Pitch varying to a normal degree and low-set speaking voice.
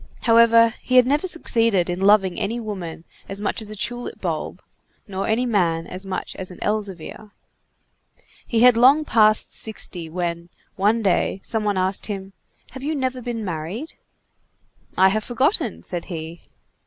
No: average, 4.0 semitones; high, 210 Hz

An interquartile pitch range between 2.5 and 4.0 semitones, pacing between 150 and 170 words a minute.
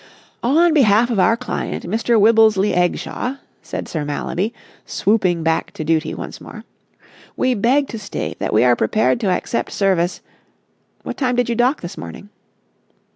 No: wide, 5.4 semitones; average, 160 wpm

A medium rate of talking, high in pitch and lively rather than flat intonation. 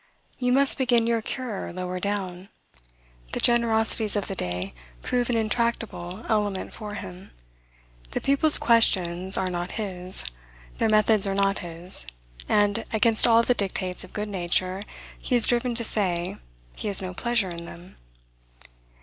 No: average, 150 wpm; high, 205 Hz; average, 4.0 semitones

